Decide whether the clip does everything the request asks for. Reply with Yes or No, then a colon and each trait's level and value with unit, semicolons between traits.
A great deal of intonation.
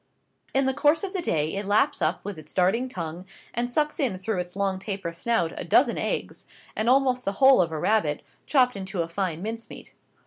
Yes: wide, 5.9 semitones